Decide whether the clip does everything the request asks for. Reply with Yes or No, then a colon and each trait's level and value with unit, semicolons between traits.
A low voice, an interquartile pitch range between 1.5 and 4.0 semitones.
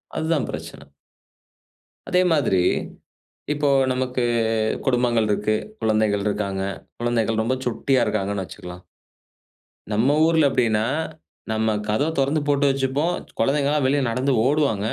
No: low, 125 Hz; average, 4.7 semitones